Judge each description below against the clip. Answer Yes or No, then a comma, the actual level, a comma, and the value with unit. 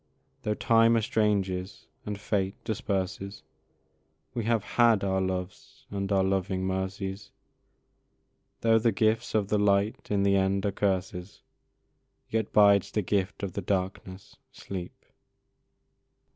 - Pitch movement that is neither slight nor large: No, narrow, 1.8 semitones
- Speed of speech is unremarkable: No, slow, 125 wpm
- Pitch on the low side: Yes, low, 100 Hz